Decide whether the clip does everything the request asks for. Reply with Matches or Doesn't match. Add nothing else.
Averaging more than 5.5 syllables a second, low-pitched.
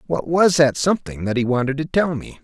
Doesn't match